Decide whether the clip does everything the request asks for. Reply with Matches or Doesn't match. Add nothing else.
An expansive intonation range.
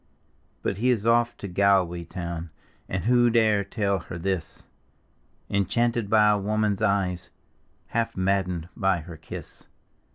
Doesn't match